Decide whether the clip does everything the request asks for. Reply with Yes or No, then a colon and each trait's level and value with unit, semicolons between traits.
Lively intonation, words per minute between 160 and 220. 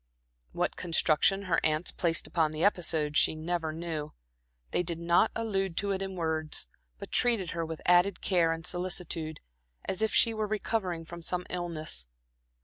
No: average, 2.9 semitones; average, 165 wpm